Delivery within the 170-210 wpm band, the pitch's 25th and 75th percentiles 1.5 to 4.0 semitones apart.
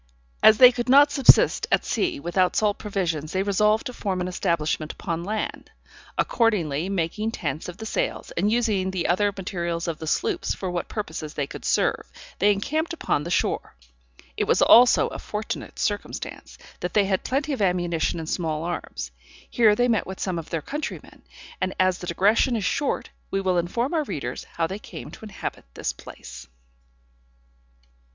No: average, 180 wpm; average, 4.4 semitones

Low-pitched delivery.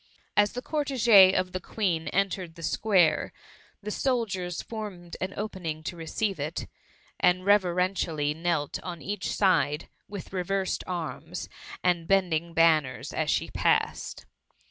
No: medium, 185 Hz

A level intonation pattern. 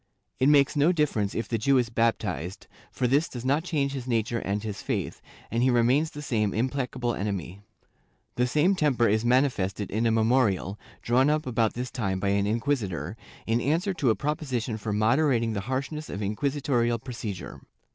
No: average, 4.3 semitones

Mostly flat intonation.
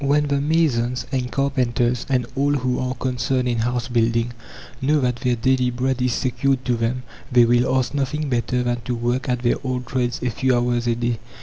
Yes: narrow, 1.5 semitones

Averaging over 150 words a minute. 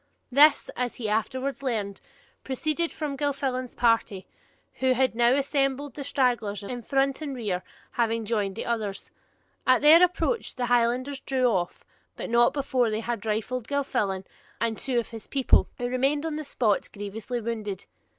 Yes: average, 160 wpm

